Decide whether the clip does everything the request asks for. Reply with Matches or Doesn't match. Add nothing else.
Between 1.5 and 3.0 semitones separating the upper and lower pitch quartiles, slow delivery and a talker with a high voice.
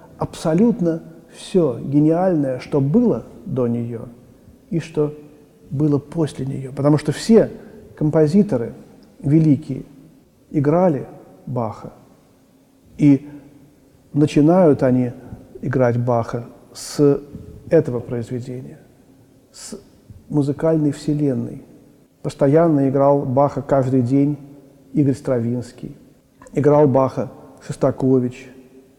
Doesn't match